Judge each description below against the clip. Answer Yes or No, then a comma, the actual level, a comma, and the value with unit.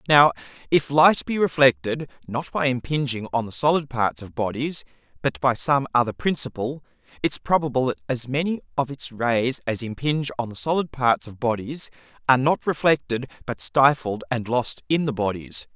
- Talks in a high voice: No, low, 130 Hz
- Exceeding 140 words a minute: Yes, average, 170 wpm